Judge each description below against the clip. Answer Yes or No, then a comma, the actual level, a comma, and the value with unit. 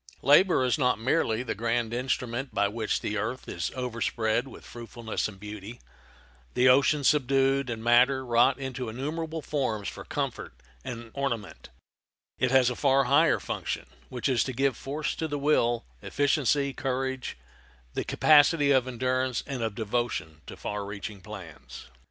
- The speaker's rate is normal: Yes, average, 155 wpm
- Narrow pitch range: No, average, 3.0 semitones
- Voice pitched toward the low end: Yes, low, 125 Hz